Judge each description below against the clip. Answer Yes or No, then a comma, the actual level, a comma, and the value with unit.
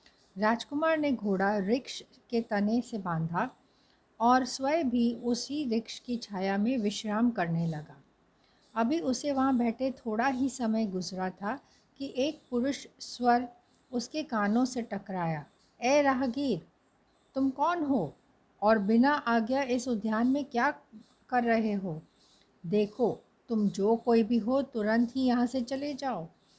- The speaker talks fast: No, average, 140 wpm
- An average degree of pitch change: Yes, average, 3.7 semitones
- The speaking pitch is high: Yes, high, 235 Hz